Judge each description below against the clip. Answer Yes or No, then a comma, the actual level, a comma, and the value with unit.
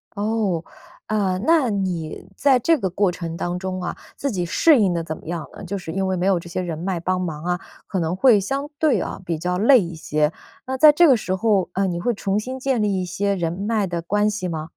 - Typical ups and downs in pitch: Yes, average, 3.7 semitones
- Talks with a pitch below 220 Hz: Yes, high, 190 Hz